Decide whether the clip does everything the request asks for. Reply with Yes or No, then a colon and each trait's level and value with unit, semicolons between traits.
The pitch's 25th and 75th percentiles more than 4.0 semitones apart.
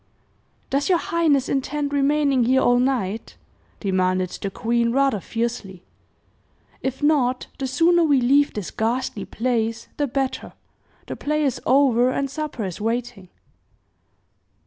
No: average, 3.7 semitones